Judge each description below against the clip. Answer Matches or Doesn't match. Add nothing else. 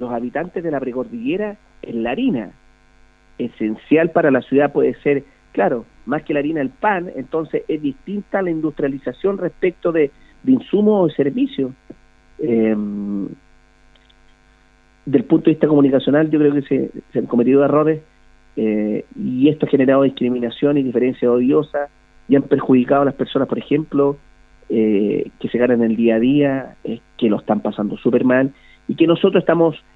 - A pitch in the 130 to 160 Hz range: Matches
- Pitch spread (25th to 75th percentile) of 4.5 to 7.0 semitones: Matches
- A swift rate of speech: Doesn't match